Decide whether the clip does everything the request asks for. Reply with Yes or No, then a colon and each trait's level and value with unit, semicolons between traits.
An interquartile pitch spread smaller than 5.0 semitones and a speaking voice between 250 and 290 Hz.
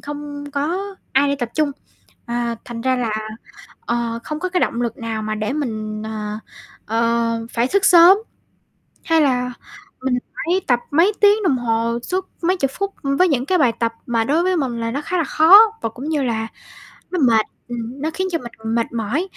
No: wide, 5.6 semitones; very high, 255 Hz